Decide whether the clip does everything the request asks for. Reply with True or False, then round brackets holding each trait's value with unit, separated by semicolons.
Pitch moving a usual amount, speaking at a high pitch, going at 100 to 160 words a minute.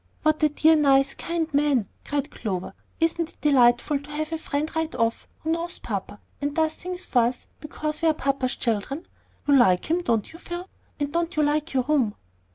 False (3.8 semitones; 295 Hz; 200 wpm)